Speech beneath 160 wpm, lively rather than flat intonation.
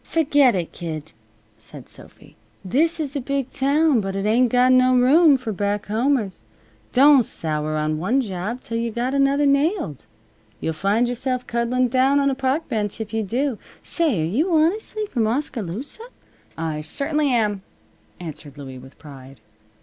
No: average, 165 wpm; wide, 6.3 semitones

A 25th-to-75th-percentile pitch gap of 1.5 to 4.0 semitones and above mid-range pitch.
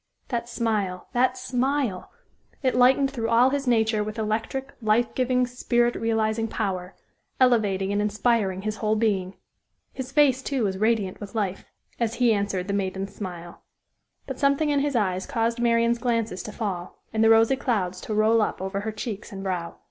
Yes: average, 3.6 semitones; high, 225 Hz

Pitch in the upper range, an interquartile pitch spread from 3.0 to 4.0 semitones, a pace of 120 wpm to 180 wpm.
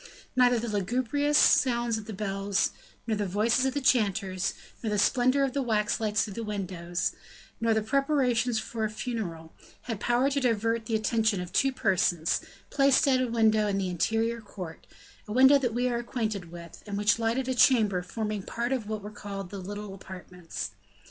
No: high, 220 Hz; average, 3.6 semitones; average, 190 wpm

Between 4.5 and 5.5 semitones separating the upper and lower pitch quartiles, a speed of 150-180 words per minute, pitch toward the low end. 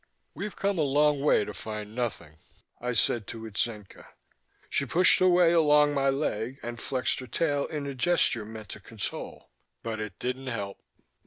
Yes: average, 5.1 semitones; average, 175 wpm; low, 125 Hz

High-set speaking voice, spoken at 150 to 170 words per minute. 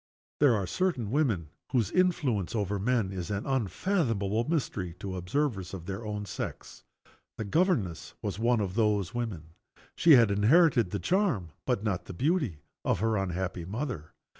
No: low, 105 Hz; average, 160 wpm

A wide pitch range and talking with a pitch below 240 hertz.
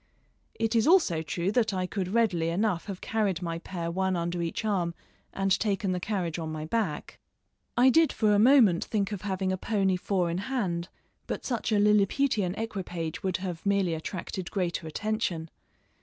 No: average, 3.8 semitones; high, 190 Hz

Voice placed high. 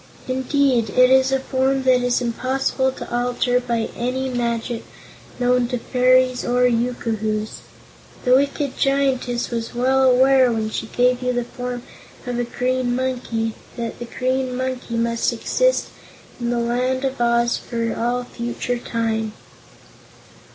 Yes: high, 245 Hz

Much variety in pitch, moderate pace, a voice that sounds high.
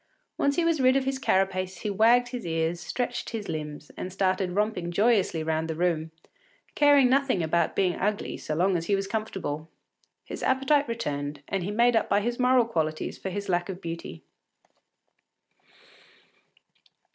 Yes: wide, 6.2 semitones; average, 170 wpm; high, 195 Hz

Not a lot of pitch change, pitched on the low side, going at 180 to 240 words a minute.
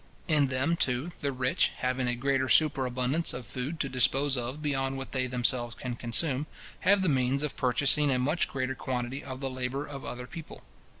Yes: narrow, 2.1 semitones; low, 130 Hz; average, 190 wpm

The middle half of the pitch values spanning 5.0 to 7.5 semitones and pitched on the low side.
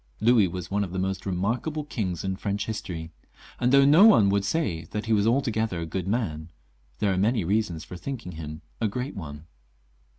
No: average, 4.3 semitones; low, 100 Hz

